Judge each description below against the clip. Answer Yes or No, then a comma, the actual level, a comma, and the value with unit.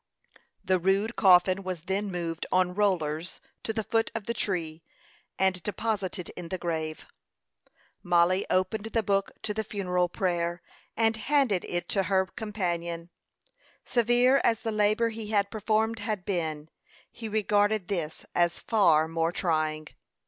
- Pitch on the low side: No, high, 190 Hz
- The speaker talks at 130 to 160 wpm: Yes, average, 145 wpm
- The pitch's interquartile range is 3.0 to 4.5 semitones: Yes, average, 3.8 semitones